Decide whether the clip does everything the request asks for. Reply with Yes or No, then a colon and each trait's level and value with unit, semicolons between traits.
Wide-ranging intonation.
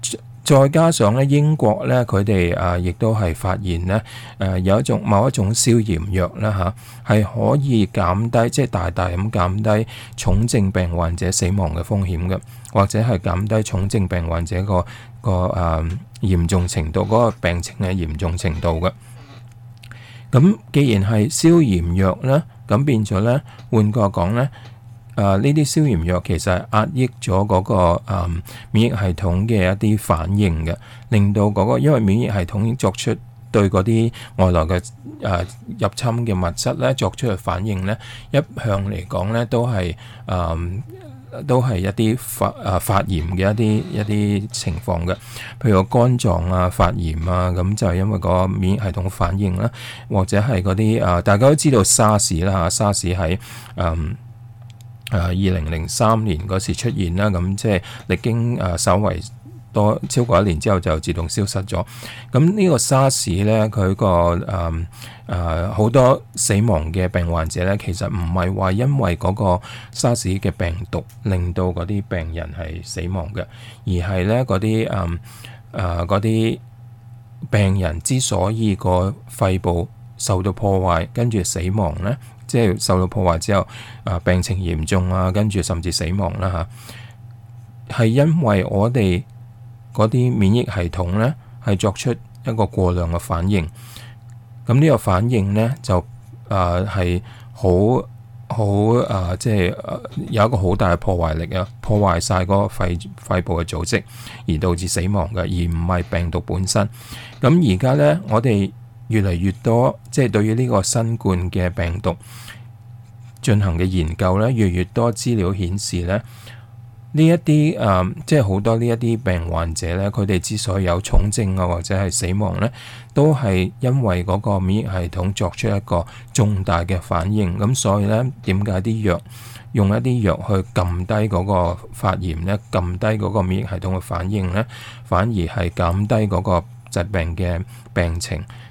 No: average, 4.3 semitones